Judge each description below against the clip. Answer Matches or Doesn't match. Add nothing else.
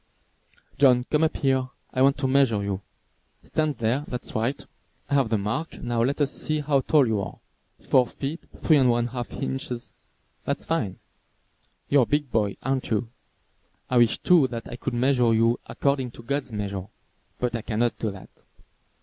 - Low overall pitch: Matches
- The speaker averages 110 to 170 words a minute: Doesn't match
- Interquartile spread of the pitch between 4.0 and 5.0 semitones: Doesn't match